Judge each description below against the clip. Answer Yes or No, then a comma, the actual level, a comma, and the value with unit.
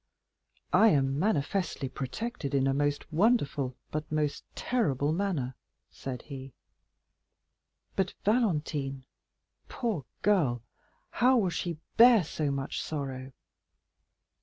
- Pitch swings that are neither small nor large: No, wide, 6.7 semitones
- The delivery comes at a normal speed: No, slow, 105 wpm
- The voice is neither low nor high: Yes, medium, 150 Hz